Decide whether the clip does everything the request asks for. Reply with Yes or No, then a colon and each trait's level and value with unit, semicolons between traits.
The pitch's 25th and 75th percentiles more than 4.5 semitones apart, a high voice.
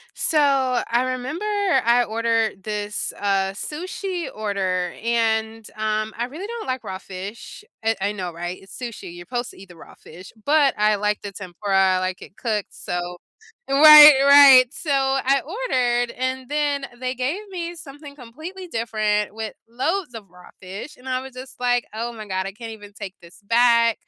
Yes: average, 5.1 semitones; high, 235 Hz